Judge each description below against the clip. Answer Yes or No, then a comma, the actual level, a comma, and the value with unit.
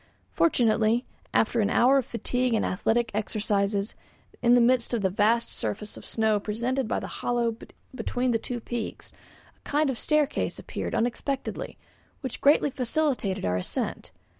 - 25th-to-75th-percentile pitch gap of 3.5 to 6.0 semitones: No, average, 2.9 semitones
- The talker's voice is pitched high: Yes, high, 235 Hz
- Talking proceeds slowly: No, average, 155 wpm